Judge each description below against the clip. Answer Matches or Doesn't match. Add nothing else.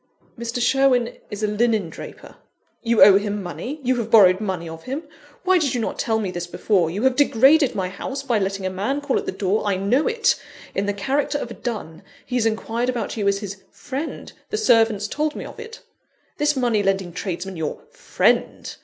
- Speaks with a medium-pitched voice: Doesn't match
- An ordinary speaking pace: Doesn't match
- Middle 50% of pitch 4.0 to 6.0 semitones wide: Matches